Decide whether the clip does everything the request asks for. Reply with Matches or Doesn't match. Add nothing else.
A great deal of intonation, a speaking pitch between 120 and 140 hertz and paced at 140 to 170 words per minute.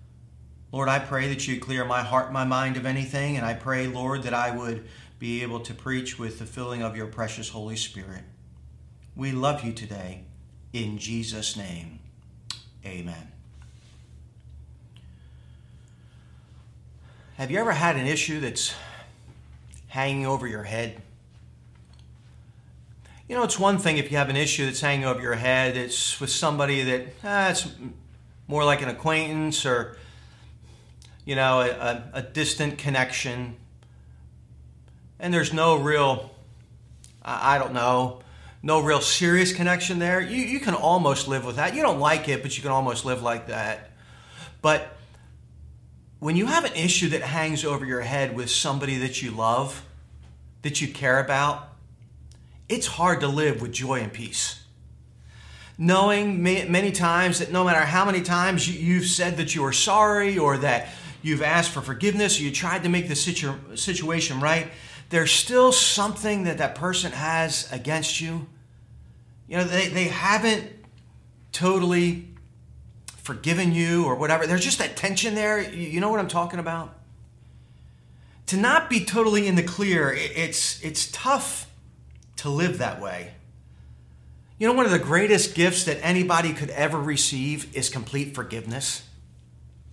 Matches